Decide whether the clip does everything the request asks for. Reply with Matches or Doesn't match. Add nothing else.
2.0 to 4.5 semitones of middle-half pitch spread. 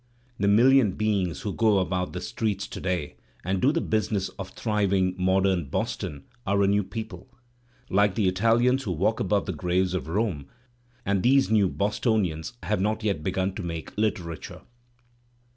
Matches